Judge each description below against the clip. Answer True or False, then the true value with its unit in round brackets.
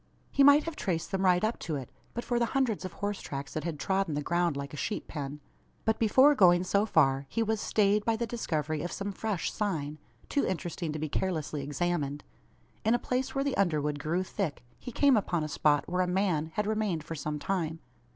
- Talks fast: True (220 wpm)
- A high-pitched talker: False (180 Hz)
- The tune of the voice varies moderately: False (5.9 semitones)